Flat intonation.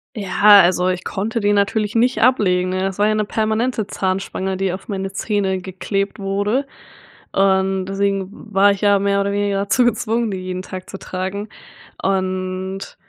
Yes: narrow, 1.6 semitones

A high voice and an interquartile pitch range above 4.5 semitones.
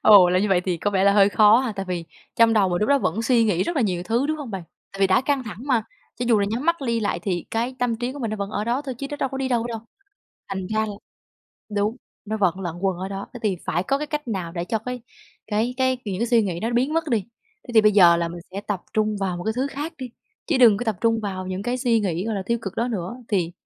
No: high, 215 Hz; average, 4.2 semitones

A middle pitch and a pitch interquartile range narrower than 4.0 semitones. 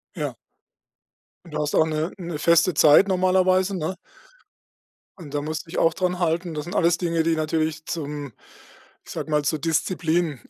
Yes: medium, 165 Hz; narrow, 2.5 semitones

